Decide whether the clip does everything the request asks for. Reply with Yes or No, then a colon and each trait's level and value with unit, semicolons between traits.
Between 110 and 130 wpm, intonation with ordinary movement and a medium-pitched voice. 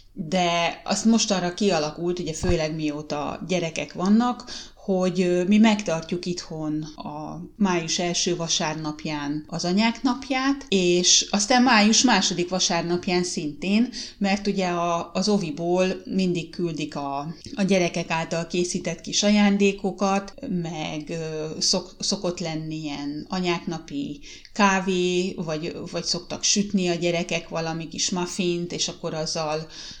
Yes: average, 120 wpm; average, 3.2 semitones; medium, 175 Hz